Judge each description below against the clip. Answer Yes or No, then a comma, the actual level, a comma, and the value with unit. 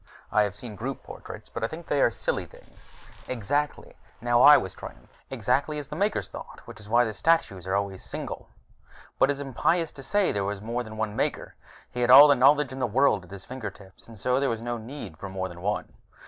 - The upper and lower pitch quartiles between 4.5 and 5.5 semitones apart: Yes, average, 5.2 semitones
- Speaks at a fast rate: Yes, fast, 235 wpm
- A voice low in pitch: Yes, low, 120 Hz